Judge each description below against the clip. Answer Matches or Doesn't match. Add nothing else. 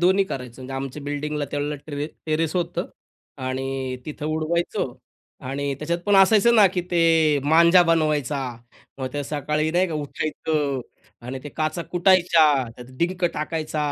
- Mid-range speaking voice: Matches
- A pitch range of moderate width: Matches